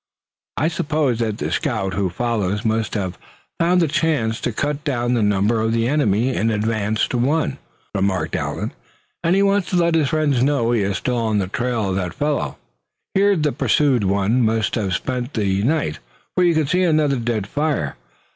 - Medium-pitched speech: No, low, 120 Hz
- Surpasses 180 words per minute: Yes, average, 195 wpm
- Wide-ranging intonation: Yes, wide, 6.2 semitones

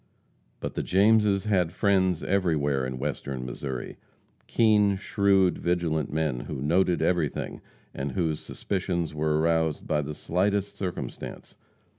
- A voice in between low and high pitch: No, very low, 85 Hz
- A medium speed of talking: No, slow, 125 wpm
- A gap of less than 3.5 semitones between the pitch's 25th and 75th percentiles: No, average, 4.6 semitones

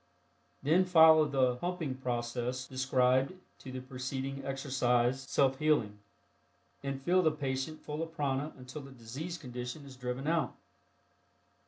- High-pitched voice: No, low, 135 Hz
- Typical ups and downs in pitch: Yes, average, 3.1 semitones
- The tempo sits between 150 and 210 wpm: No, slow, 135 wpm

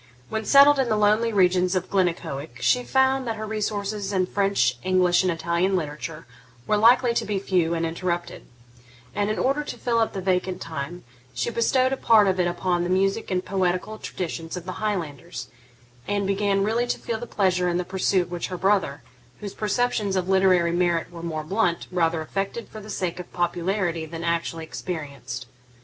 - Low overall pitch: No, medium, 185 Hz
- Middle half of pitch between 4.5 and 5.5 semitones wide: No, average, 3.5 semitones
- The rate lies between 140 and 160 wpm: No, average, 190 wpm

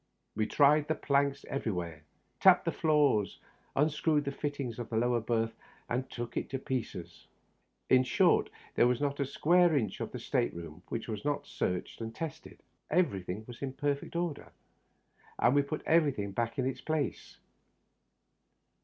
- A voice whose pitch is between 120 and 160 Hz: Yes, low, 135 Hz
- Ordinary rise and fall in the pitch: Yes, average, 4.4 semitones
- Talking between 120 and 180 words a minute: Yes, average, 170 wpm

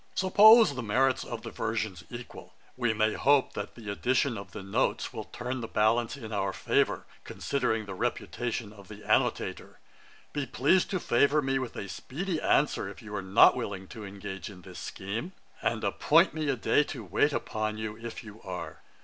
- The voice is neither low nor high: No, low, 115 Hz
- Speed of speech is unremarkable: Yes, average, 190 wpm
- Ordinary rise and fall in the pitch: Yes, average, 4.5 semitones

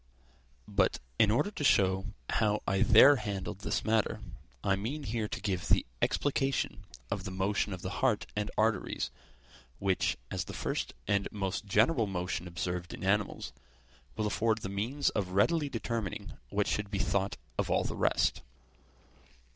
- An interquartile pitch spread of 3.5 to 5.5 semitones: No, average, 2.7 semitones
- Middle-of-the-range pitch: No, low, 105 Hz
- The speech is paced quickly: No, average, 160 wpm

